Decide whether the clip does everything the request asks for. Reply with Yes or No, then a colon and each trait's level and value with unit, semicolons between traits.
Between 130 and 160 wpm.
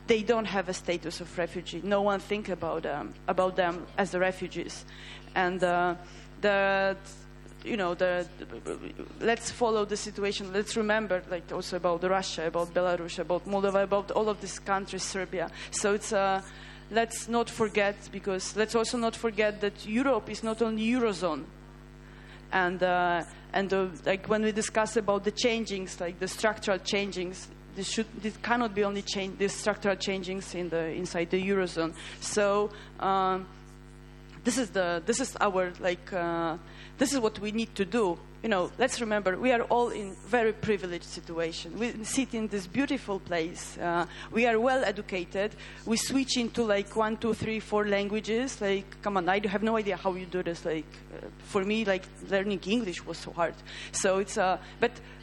No: average, 180 wpm